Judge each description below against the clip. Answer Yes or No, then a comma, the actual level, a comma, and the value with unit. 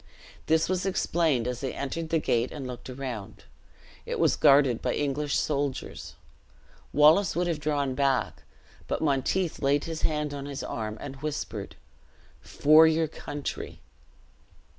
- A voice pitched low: No, medium, 145 Hz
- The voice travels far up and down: No, average, 3.0 semitones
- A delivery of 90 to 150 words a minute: Yes, average, 140 wpm